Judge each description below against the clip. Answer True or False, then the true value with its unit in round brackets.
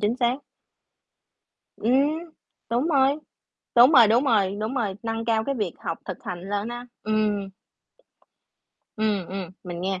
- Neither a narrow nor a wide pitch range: True (3.8 semitones)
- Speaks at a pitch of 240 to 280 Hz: False (220 Hz)